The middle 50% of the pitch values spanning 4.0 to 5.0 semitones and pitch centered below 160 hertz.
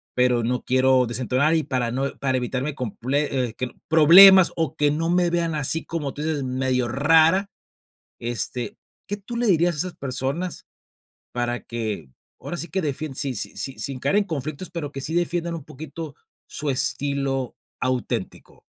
Yes: average, 4.4 semitones; medium, 140 Hz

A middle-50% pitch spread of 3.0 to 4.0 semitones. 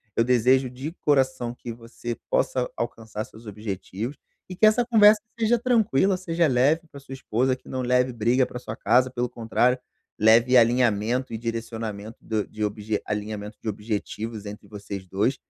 Yes: average, 3.4 semitones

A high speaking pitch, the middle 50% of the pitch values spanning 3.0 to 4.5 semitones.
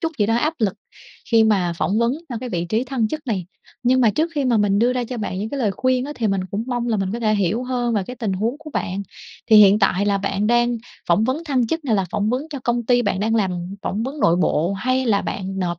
Yes: high, 225 Hz; average, 4.0 semitones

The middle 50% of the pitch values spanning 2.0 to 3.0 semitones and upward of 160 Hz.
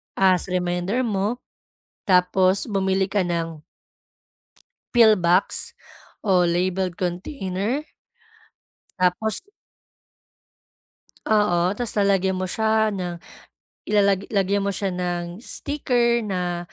Yes: average, 2.7 semitones; high, 190 Hz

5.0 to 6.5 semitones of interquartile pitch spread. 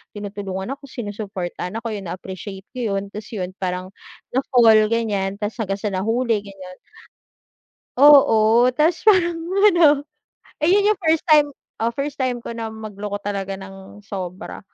Yes: average, 5.3 semitones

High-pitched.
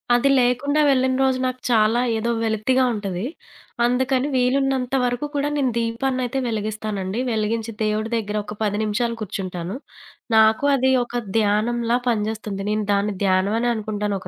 Yes: high, 225 Hz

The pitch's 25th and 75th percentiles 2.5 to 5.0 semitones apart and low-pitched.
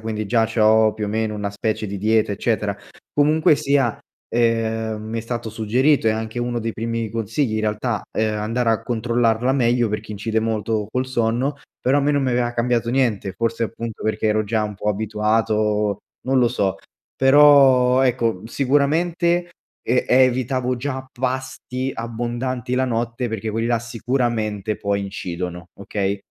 Yes: average, 2.8 semitones; low, 115 Hz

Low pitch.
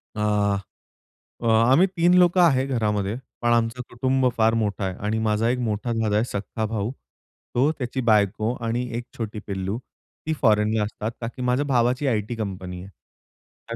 Yes: low, 115 Hz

